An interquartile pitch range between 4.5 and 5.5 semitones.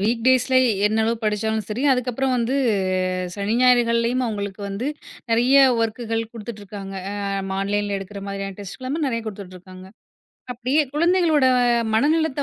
No: average, 3.9 semitones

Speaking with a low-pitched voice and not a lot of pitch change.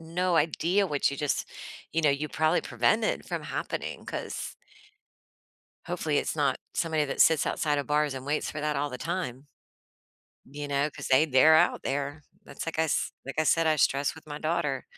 No: medium, 150 Hz; narrow, 2.3 semitones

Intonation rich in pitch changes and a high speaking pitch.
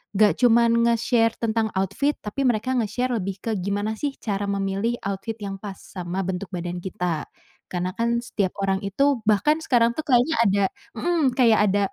No: average, 3.4 semitones; high, 215 Hz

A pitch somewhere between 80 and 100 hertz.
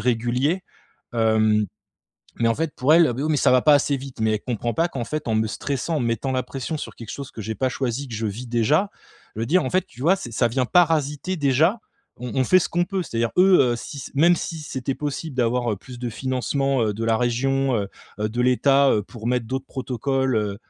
No: low, 130 Hz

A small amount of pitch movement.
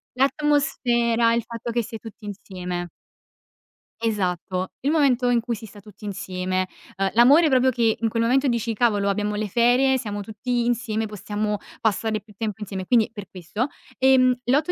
No: average, 3.1 semitones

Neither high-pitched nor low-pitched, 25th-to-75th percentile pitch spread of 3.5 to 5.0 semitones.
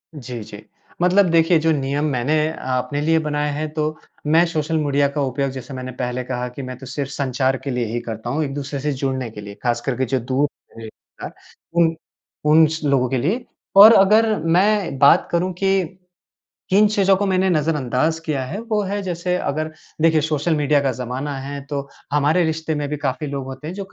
Yes: medium, 150 Hz; average, 3.8 semitones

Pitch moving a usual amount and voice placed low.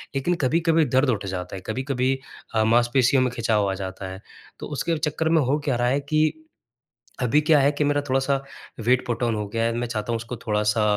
Yes: average, 4.4 semitones; low, 125 Hz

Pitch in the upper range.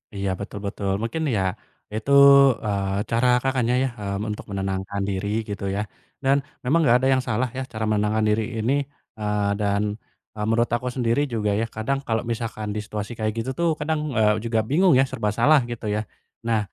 No: low, 110 Hz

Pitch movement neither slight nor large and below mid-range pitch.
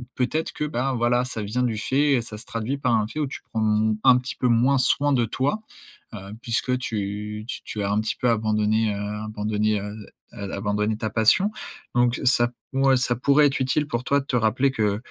Yes: average, 3.4 semitones; low, 120 Hz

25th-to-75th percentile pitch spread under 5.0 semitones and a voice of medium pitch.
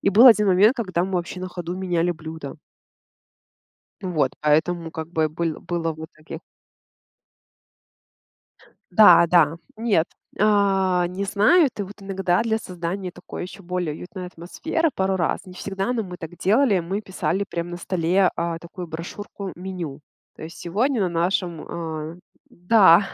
Yes: average, 2.8 semitones; medium, 180 Hz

